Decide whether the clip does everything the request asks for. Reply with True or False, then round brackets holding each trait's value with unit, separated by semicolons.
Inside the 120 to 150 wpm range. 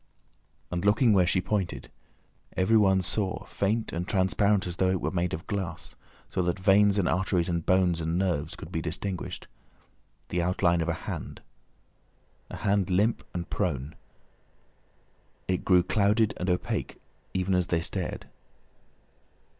True (145 wpm)